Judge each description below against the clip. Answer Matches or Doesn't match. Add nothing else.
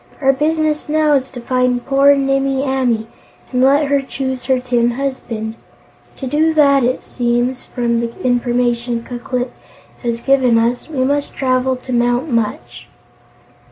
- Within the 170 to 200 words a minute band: Doesn't match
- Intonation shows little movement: Matches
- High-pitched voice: Matches